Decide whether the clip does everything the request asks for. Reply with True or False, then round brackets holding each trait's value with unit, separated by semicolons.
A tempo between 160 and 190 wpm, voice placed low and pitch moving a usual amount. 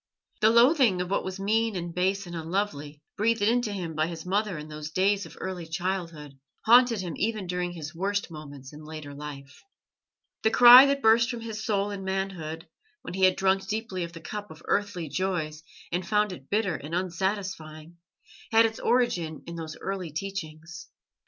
False (185 wpm; 185 Hz; 4.5 semitones)